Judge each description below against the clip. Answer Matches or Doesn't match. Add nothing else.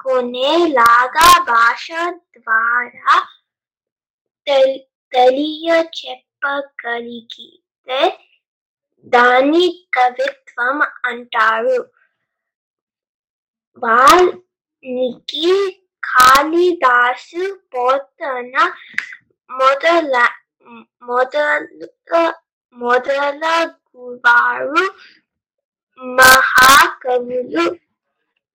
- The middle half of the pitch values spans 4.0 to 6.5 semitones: Matches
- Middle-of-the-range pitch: Doesn't match